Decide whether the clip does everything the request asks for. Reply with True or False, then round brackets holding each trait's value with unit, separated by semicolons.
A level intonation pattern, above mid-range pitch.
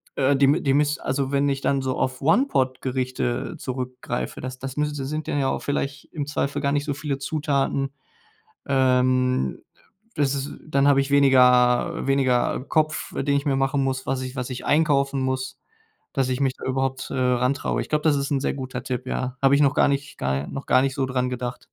False (1.6 semitones; 135 Hz)